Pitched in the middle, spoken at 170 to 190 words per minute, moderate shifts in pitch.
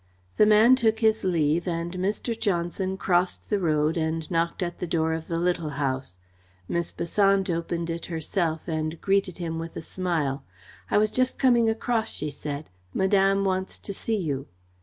Yes: medium, 175 Hz; average, 175 wpm; average, 3.5 semitones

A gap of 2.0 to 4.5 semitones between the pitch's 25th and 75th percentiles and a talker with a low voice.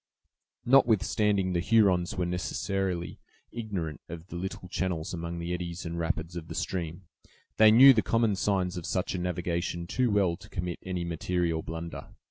Yes: narrow, 2.5 semitones; very low, 90 Hz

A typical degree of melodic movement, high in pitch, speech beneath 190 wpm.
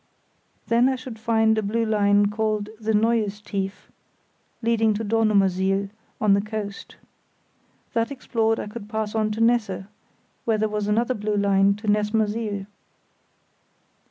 No: narrow, 1.6 semitones; high, 215 Hz; average, 140 wpm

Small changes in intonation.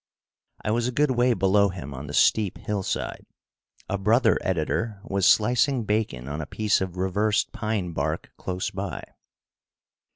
No: average, 3.6 semitones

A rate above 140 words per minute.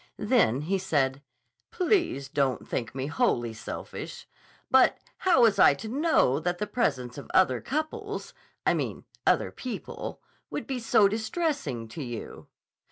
No: slow, 135 wpm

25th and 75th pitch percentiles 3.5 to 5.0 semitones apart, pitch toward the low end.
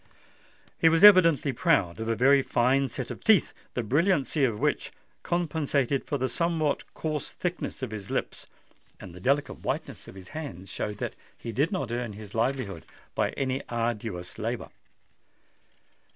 No: wide, 5.4 semitones; low, 130 Hz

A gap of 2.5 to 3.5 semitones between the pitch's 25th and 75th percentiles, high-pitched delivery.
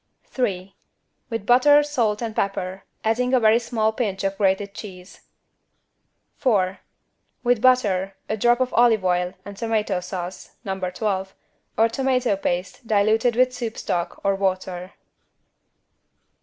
No: average, 3.9 semitones; high, 210 Hz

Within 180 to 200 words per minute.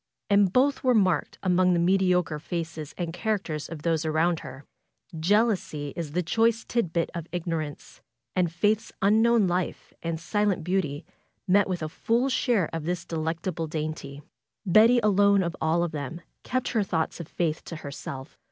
No: average, 165 wpm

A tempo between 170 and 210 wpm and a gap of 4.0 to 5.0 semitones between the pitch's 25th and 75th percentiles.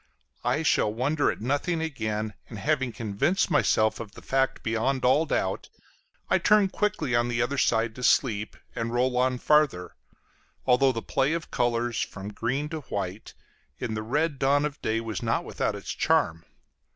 Yes: average, 175 wpm; average, 4.3 semitones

